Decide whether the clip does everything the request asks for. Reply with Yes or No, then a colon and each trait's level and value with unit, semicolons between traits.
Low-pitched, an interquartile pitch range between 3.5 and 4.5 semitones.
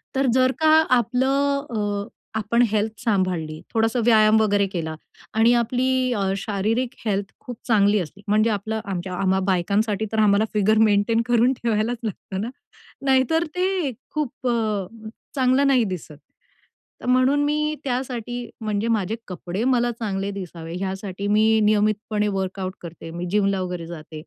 No: high, 215 Hz; average, 3.8 semitones